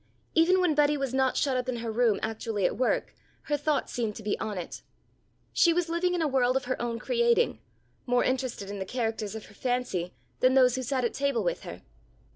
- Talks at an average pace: No, fast, 225 wpm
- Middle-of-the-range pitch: No, very high, 255 Hz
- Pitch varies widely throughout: No, average, 4.5 semitones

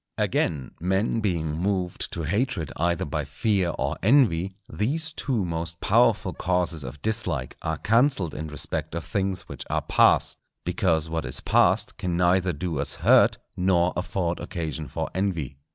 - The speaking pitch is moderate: No, very low, 85 Hz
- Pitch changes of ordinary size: Yes, average, 3.8 semitones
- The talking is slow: No, average, 155 wpm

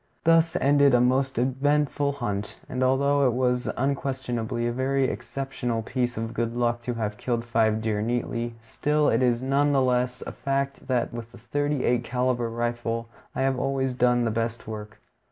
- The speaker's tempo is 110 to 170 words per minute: No, average, 180 wpm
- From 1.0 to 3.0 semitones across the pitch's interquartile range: Yes, narrow, 2.5 semitones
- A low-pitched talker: Yes, low, 125 Hz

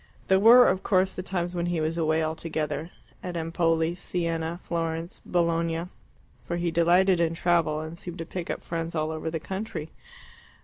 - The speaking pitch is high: No, medium, 170 Hz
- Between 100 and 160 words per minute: No, average, 175 wpm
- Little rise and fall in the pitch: Yes, narrow, 1.4 semitones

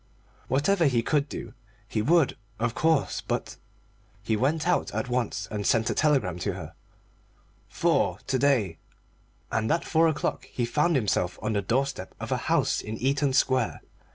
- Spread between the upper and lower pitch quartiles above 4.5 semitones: Yes, average, 5.1 semitones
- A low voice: Yes, low, 130 Hz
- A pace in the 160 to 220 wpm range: Yes, average, 165 wpm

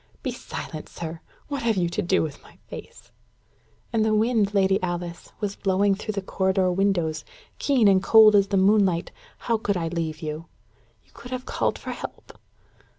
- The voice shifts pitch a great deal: No, average, 3.6 semitones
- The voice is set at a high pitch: Yes, high, 195 Hz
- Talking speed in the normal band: Yes, average, 180 wpm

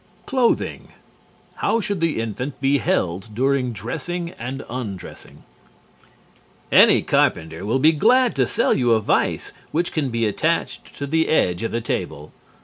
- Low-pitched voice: Yes, low, 130 Hz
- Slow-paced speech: No, average, 145 wpm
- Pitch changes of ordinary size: No, wide, 6.3 semitones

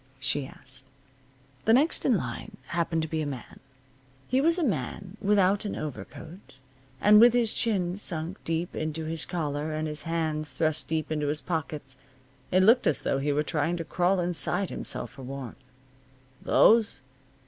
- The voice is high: No, medium, 160 Hz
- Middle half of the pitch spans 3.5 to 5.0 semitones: Yes, average, 4.7 semitones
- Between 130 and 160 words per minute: No, average, 170 wpm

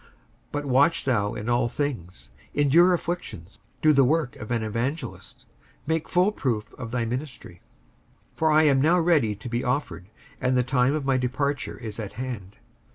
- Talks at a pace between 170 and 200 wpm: Yes, average, 180 wpm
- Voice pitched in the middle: No, low, 130 Hz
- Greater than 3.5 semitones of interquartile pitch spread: Yes, average, 4.5 semitones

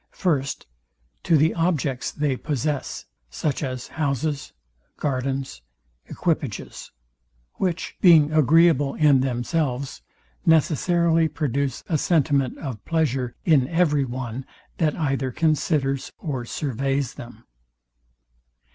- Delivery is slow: Yes, slow, 100 wpm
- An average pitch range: Yes, average, 3.3 semitones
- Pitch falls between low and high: Yes, medium, 145 Hz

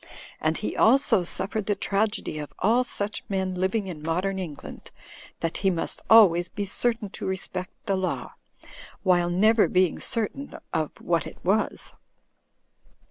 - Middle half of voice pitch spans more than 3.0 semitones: Yes, average, 3.4 semitones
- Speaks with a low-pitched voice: No, high, 190 Hz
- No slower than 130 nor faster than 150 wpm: Yes, average, 145 wpm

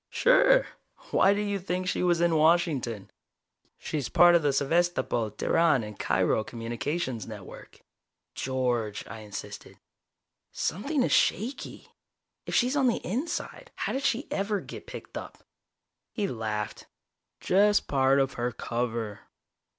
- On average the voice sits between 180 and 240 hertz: No, medium, 155 Hz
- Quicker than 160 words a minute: No, slow, 135 wpm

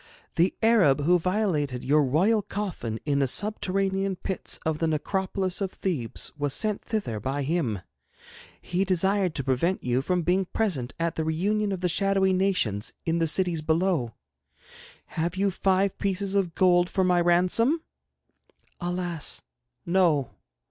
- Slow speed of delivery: No, average, 150 wpm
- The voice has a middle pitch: Yes, medium, 180 Hz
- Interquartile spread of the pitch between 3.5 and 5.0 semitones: Yes, average, 4.1 semitones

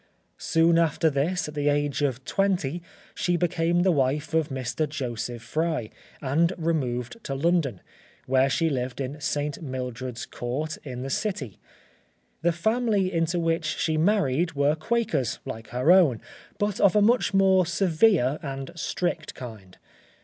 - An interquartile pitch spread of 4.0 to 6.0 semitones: Yes, average, 4.8 semitones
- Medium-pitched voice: Yes, medium, 155 Hz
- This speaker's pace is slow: No, average, 150 wpm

